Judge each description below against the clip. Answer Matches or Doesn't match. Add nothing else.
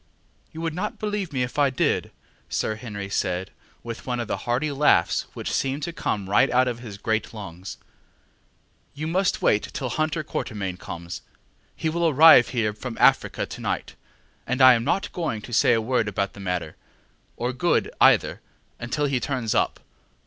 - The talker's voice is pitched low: Matches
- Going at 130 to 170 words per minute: Doesn't match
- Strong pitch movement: Matches